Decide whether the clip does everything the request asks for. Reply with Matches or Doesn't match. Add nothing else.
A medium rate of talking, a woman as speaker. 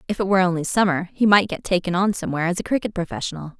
Doesn't match